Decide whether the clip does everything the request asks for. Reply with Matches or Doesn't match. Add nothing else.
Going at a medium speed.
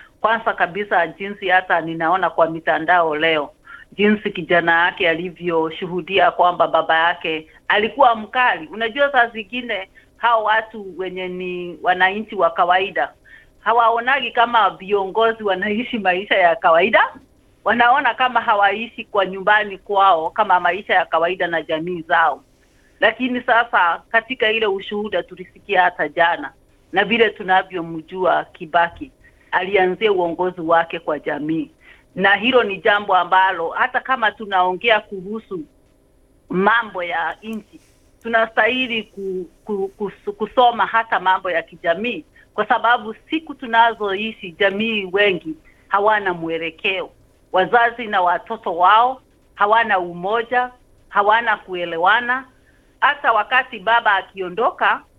Matches